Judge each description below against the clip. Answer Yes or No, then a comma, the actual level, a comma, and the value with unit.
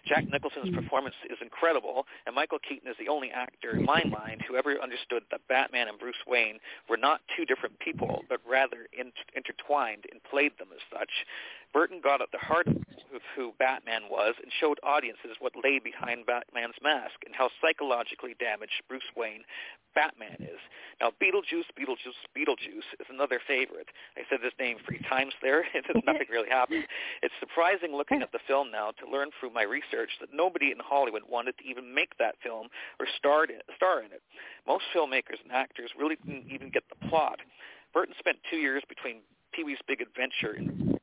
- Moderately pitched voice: Yes, medium, 150 Hz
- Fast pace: No, average, 185 wpm